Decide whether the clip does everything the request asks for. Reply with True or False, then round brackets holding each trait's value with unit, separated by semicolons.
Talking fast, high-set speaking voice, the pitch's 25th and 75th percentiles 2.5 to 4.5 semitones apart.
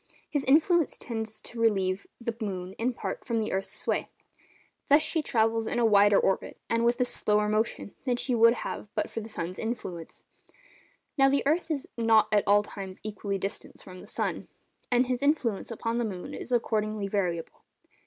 False (185 wpm; 225 Hz; 3.2 semitones)